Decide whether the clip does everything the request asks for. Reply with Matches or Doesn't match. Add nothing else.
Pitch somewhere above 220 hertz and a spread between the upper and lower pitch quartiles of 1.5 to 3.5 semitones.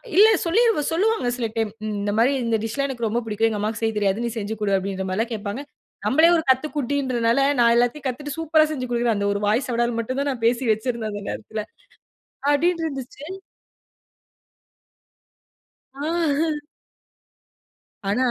Doesn't match